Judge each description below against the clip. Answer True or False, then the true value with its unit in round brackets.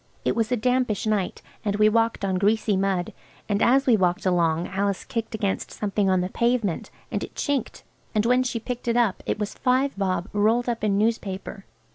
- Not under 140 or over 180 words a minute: False (200 wpm)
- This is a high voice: True (210 Hz)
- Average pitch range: True (3.2 semitones)